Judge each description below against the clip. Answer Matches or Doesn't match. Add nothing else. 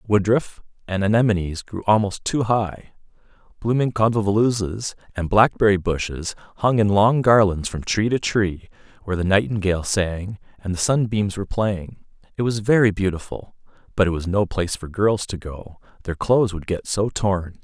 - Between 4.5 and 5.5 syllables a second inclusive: Matches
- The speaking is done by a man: Matches